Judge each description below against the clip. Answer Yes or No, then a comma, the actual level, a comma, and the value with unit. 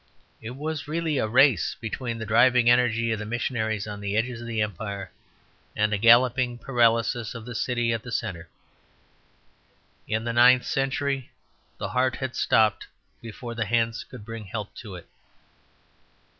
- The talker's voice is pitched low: Yes, low, 115 Hz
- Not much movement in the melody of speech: Yes, narrow, 2.3 semitones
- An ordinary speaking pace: Yes, average, 160 wpm